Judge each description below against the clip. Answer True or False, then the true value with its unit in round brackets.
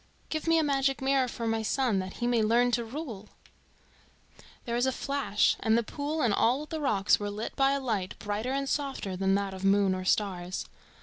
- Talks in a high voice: True (235 Hz)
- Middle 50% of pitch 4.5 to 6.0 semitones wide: True (5.1 semitones)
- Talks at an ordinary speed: False (210 wpm)